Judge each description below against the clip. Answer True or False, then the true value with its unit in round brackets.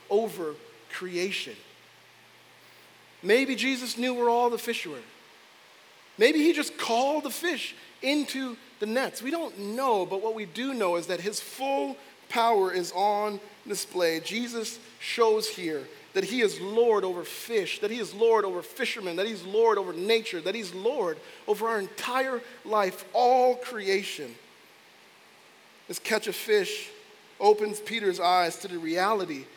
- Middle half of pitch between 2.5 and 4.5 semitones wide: False (5.1 semitones)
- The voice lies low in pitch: False (230 Hz)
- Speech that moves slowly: False (150 wpm)